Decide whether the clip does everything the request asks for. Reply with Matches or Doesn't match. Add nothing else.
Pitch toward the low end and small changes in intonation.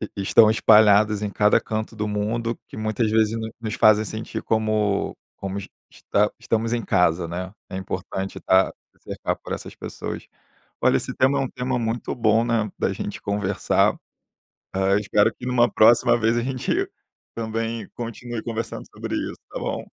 Matches